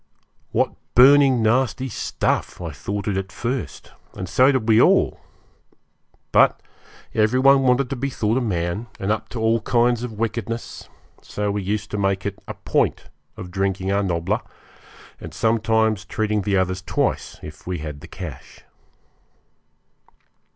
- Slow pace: No, average, 150 wpm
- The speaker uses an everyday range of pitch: Yes, average, 3.7 semitones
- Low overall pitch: Yes, low, 110 Hz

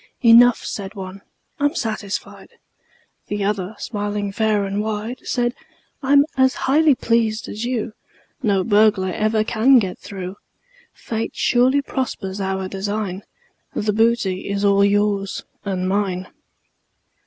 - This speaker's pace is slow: Yes, slow, 125 wpm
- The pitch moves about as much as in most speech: Yes, average, 3.0 semitones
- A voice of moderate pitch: No, high, 210 Hz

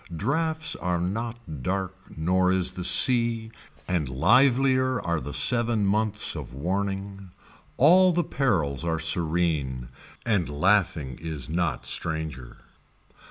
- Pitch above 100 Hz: No, very low, 95 Hz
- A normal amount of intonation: No, wide, 6.5 semitones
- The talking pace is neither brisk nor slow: No, slow, 115 wpm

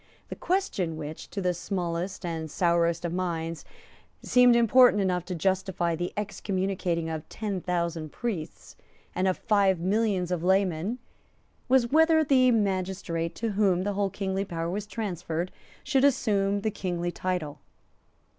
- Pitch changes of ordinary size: Yes, average, 3.4 semitones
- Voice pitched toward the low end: No, medium, 185 Hz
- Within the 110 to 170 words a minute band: Yes, average, 145 wpm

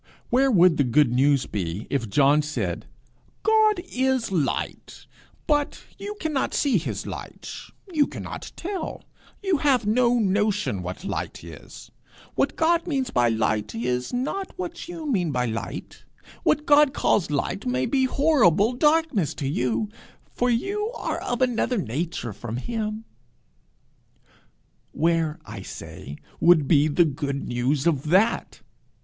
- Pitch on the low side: No, high, 195 Hz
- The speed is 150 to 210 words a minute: No, average, 140 wpm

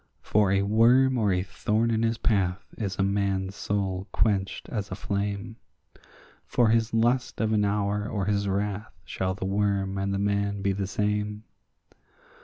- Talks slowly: No, average, 170 wpm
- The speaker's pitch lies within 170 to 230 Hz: No, low, 100 Hz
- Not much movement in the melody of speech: Yes, narrow, 1.8 semitones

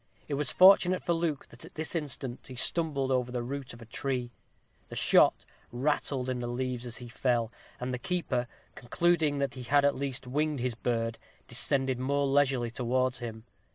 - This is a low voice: Yes, low, 130 Hz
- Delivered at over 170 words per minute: Yes, average, 190 wpm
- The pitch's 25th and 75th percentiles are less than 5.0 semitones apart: Yes, average, 2.7 semitones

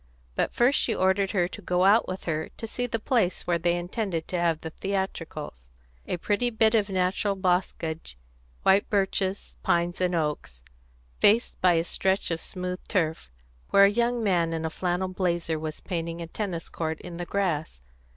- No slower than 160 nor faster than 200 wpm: Yes, average, 180 wpm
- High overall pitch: No, medium, 180 Hz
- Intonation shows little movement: No, average, 3.1 semitones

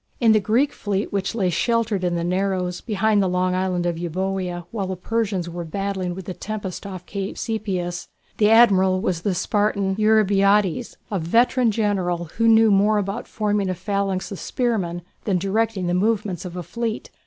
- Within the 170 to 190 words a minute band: Yes, average, 180 wpm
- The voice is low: No, high, 195 Hz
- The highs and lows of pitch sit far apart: No, average, 3.0 semitones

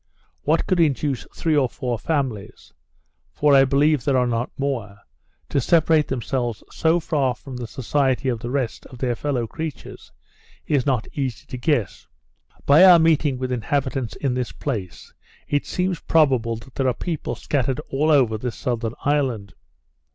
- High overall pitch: No, low, 135 Hz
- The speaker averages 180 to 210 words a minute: No, average, 165 wpm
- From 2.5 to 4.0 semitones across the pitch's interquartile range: Yes, average, 3.4 semitones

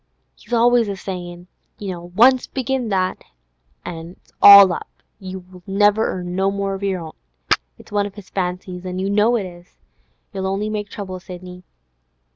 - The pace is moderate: Yes, average, 165 wpm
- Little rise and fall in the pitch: Yes, narrow, 2.3 semitones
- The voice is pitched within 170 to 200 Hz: Yes, high, 190 Hz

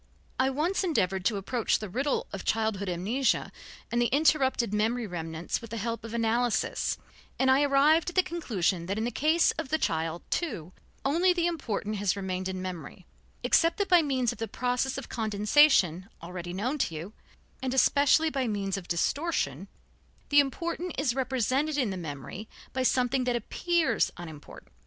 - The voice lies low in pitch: No, high, 240 Hz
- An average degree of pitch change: No, wide, 6.5 semitones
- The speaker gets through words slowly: No, average, 175 wpm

